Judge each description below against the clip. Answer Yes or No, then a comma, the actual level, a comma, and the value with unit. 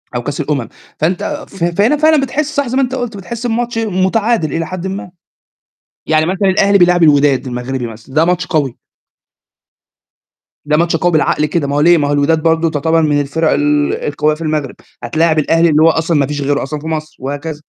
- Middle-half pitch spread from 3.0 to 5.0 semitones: Yes, average, 4.2 semitones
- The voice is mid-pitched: Yes, medium, 160 Hz